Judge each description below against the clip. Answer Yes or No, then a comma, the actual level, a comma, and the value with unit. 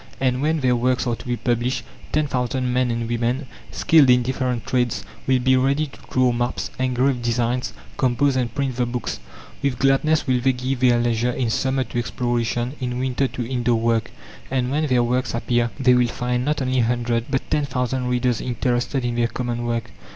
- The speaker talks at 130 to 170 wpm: No, average, 200 wpm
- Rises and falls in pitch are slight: Yes, narrow, 1.5 semitones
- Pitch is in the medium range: No, low, 125 Hz